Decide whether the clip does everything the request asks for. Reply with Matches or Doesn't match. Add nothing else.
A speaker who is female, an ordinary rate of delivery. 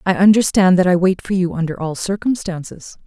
Matches